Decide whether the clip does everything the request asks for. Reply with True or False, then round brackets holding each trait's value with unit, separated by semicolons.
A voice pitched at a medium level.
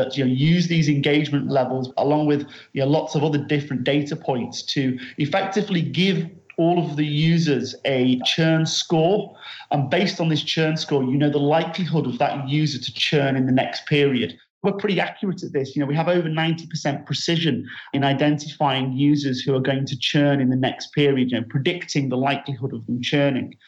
True (145 Hz)